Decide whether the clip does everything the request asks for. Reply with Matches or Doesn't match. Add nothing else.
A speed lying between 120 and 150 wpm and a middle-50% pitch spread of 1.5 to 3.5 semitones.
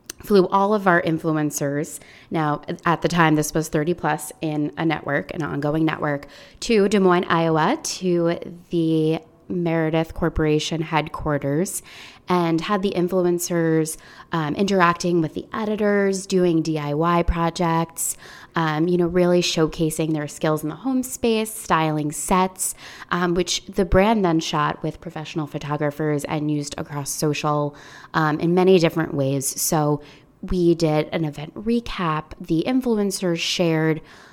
Matches